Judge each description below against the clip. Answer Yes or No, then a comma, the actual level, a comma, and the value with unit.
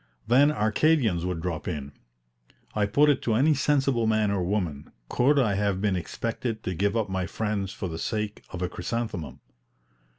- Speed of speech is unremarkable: Yes, average, 175 wpm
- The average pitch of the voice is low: Yes, low, 105 Hz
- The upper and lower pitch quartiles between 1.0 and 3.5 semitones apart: No, average, 4.6 semitones